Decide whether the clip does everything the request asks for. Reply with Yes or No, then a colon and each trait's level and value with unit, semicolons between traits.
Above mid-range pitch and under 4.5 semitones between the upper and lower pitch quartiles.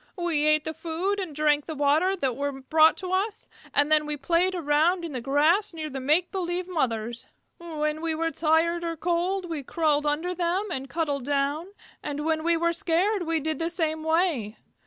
Yes: very high, 320 Hz; average, 2.8 semitones